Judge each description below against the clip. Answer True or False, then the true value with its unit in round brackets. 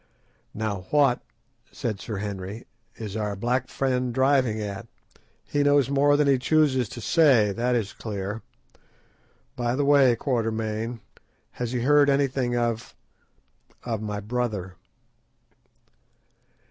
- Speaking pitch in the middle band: False (120 Hz)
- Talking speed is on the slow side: True (120 wpm)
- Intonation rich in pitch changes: False (3.9 semitones)